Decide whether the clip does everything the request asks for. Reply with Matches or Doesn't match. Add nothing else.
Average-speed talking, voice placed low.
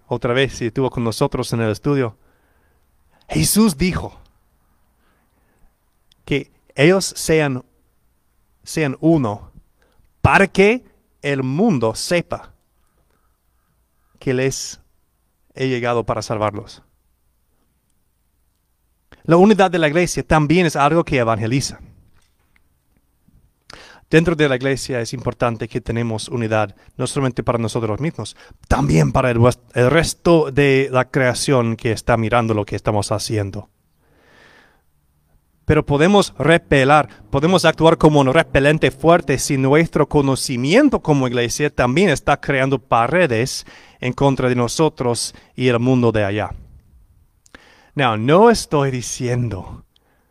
Doesn't match